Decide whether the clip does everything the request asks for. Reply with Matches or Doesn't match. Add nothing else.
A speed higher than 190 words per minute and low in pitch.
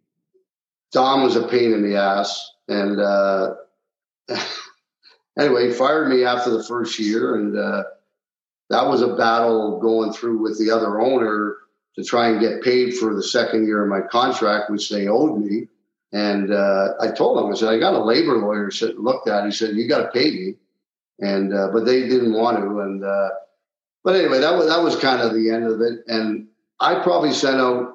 Matches